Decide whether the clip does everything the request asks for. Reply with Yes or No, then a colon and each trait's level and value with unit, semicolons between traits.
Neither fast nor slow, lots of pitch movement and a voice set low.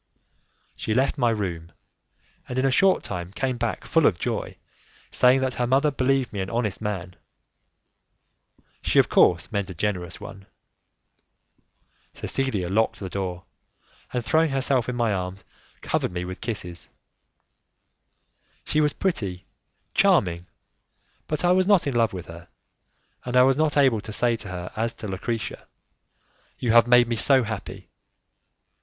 Yes: average, 155 wpm; wide, 5.9 semitones; low, 115 Hz